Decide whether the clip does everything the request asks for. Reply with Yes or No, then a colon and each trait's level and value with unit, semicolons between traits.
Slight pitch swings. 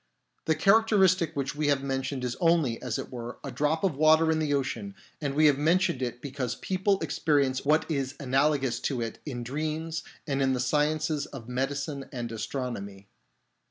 No: average, 3.5 semitones